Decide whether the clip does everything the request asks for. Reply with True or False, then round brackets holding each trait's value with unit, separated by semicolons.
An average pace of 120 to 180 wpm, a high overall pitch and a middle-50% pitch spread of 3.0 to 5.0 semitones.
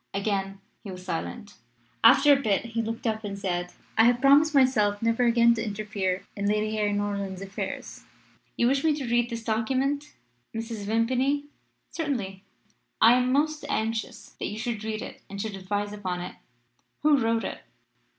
True (170 wpm; 225 Hz; 3.6 semitones)